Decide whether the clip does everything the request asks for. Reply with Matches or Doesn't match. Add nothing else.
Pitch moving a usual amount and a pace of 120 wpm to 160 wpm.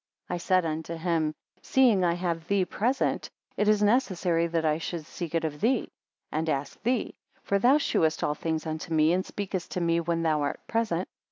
Doesn't match